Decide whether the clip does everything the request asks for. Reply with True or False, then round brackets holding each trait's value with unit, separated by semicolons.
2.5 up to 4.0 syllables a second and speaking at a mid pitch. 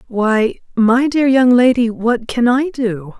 False (3.5 syllables/s; 240 Hz)